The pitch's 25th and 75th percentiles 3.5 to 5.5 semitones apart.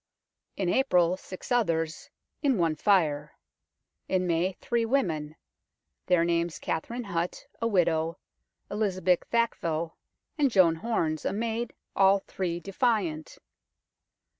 Yes: average, 5.0 semitones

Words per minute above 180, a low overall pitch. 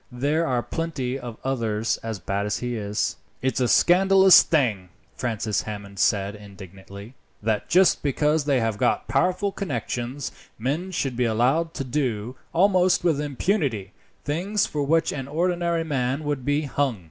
No: average, 155 wpm; low, 130 Hz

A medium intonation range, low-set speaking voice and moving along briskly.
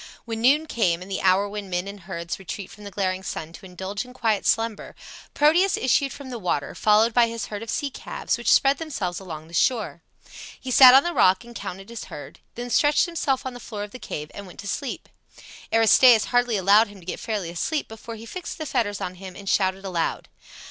No: average, 4.7 semitones; high, 210 Hz; fast, 225 wpm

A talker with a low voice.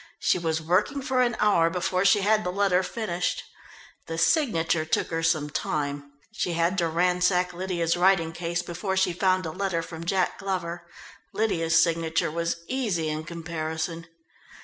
No: medium, 175 Hz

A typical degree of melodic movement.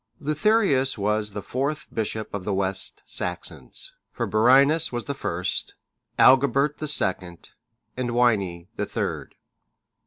No: wide, 6.1 semitones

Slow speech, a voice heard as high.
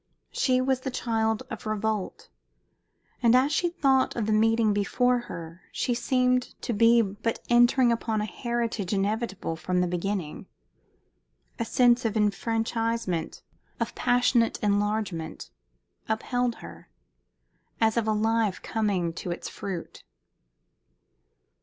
Yes: slow, 125 wpm; high, 225 Hz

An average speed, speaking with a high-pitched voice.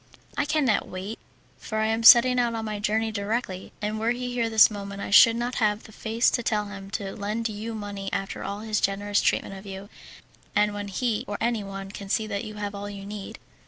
No: fast, 225 wpm; high, 210 Hz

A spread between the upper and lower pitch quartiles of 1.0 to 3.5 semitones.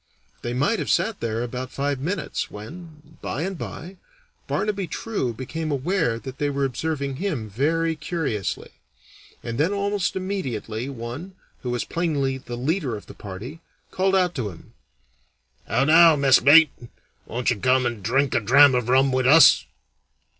No: average, 5.2 semitones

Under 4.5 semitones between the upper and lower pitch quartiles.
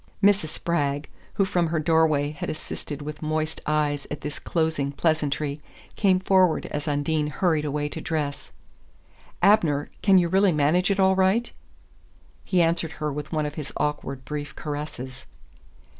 Yes: average, 2.8 semitones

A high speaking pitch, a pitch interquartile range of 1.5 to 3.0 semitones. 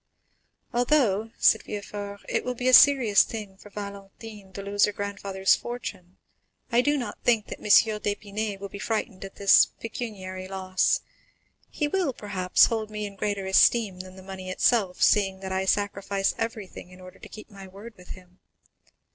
Yes: high, 200 Hz; narrow, 2.5 semitones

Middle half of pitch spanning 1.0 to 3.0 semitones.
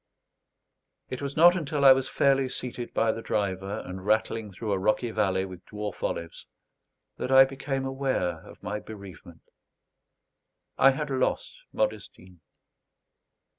No: wide, 5.6 semitones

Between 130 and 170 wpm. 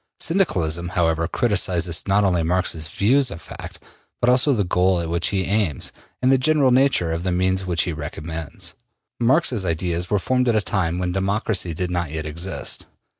No: average, 180 wpm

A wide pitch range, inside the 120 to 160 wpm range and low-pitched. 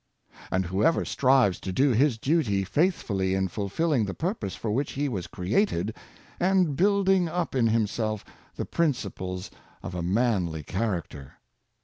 Yes: wide, 8.2 semitones; average, 140 wpm; low, 110 Hz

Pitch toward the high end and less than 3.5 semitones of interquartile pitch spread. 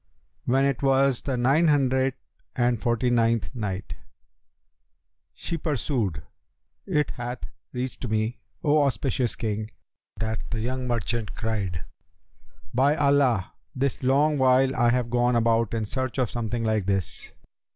No: low, 125 Hz; average, 3.0 semitones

